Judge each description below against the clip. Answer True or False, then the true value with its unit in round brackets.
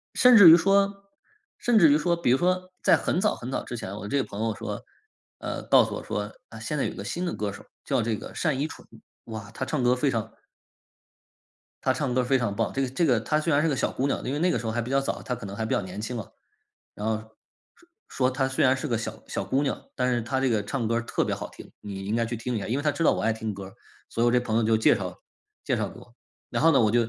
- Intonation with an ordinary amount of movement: True (4.5 semitones)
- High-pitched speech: False (125 Hz)